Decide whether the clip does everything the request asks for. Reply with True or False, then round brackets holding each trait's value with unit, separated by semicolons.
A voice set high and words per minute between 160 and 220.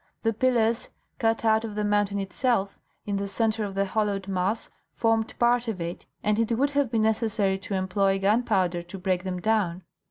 True (210 Hz; 190 wpm)